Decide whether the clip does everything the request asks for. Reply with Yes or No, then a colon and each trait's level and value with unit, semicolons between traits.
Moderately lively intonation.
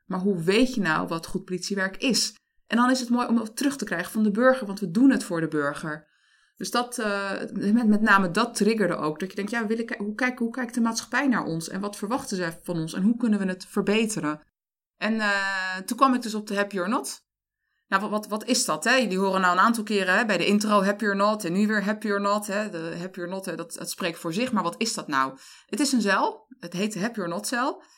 Yes: average, 3.8 semitones